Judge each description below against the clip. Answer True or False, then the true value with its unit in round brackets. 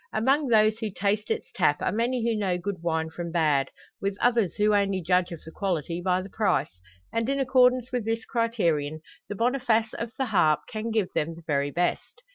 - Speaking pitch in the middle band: False (205 Hz)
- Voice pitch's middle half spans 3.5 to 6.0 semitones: True (5.2 semitones)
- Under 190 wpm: False (205 wpm)